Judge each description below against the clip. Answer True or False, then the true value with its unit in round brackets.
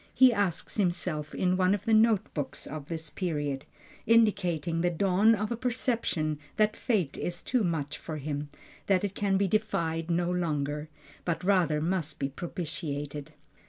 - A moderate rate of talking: True (160 wpm)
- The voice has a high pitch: False (175 Hz)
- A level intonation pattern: False (4.7 semitones)